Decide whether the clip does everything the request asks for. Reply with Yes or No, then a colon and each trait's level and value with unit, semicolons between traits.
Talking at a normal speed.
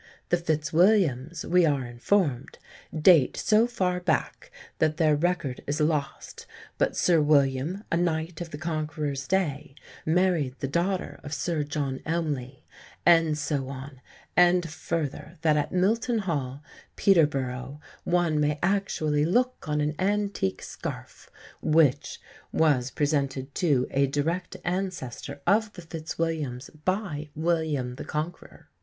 No: slow, 130 wpm